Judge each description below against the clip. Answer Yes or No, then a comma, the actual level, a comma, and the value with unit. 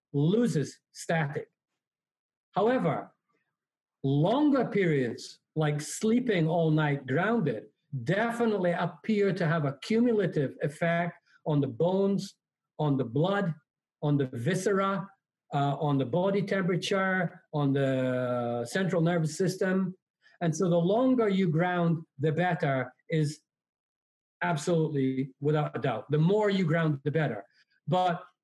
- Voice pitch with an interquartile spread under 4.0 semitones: No, average, 4.4 semitones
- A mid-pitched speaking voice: Yes, medium, 170 Hz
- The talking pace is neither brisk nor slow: No, slow, 120 wpm